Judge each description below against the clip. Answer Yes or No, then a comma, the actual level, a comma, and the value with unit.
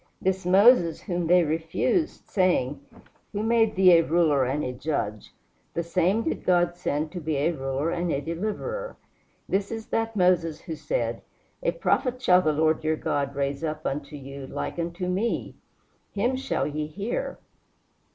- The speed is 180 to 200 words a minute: No, average, 165 wpm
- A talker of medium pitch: Yes, medium, 170 Hz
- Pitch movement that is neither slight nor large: Yes, average, 4.7 semitones